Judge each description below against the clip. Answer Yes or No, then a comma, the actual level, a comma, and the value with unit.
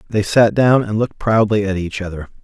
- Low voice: Yes, low, 105 Hz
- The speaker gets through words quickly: Yes, fast, 220 wpm